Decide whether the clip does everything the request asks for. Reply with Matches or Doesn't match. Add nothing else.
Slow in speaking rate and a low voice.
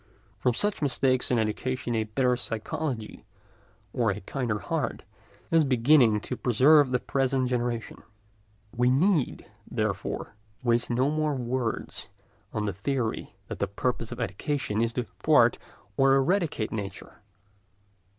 Matches